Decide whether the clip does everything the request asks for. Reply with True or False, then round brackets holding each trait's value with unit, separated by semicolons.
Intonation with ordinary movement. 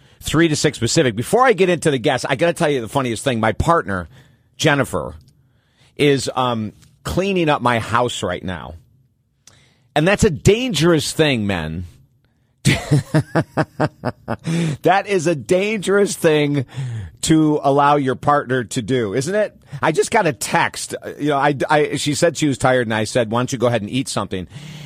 True (4.5 semitones)